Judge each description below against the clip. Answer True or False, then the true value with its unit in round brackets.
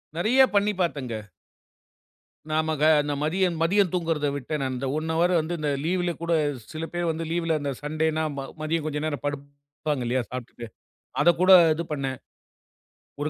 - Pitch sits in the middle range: True (155 Hz)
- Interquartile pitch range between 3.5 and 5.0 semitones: False (2.8 semitones)